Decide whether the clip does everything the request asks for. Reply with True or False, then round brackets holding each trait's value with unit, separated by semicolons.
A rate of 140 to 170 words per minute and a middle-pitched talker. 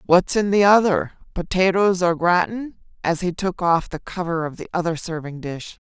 False (185 wpm; 180 Hz)